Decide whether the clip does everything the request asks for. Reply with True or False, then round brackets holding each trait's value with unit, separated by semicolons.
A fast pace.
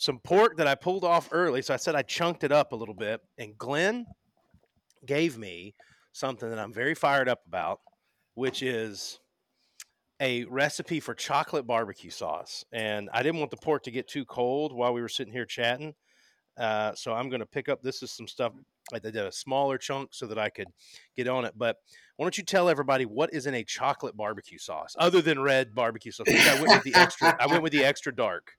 True (220 wpm)